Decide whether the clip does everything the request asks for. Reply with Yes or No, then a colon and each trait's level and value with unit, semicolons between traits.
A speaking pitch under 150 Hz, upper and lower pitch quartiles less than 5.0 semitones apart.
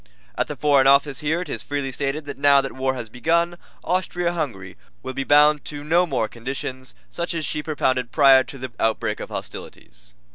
Yes: medium, 140 Hz; average, 2.9 semitones